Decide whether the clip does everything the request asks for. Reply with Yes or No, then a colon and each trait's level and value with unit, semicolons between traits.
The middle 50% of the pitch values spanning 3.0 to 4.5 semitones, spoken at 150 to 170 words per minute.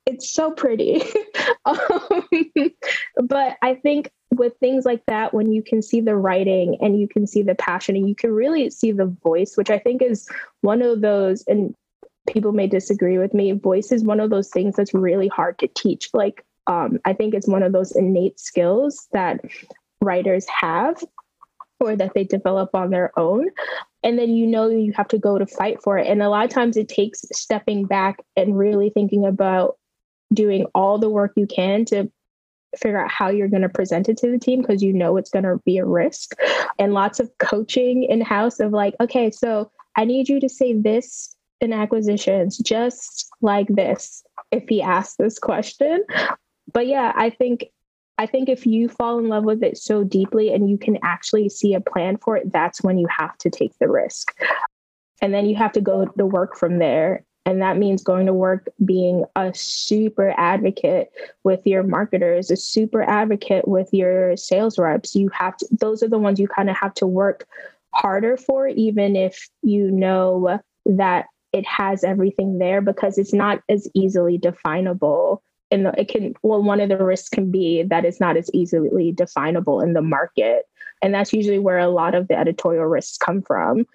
No: average, 3.4 semitones; average, 195 wpm